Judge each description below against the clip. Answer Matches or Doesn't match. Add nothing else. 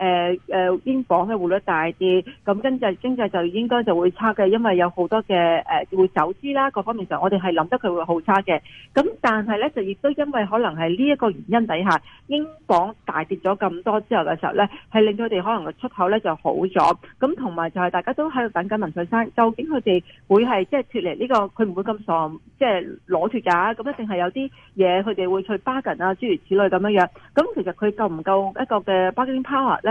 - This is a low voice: Doesn't match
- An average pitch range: Matches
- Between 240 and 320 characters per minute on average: Doesn't match